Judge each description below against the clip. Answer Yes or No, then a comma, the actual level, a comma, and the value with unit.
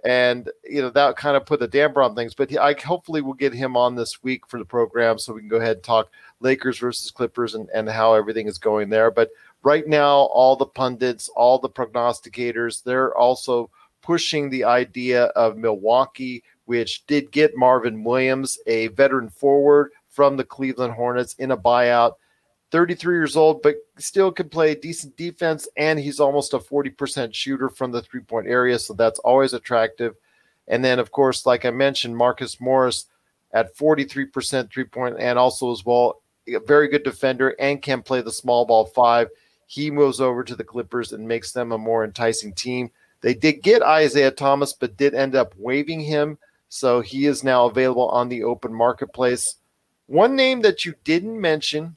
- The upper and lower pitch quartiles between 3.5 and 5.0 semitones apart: No, average, 2.9 semitones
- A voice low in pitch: Yes, low, 130 Hz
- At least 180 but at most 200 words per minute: Yes, average, 185 wpm